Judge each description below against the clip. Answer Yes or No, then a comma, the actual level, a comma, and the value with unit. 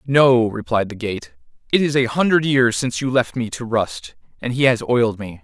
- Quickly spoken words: Yes, fast, 220 wpm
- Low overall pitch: Yes, low, 125 Hz